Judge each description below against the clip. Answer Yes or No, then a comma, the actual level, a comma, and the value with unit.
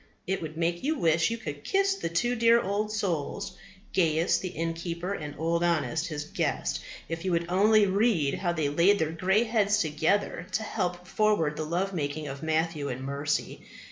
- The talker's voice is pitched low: No, medium, 170 Hz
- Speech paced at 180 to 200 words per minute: Yes, average, 185 wpm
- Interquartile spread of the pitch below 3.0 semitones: No, average, 4.3 semitones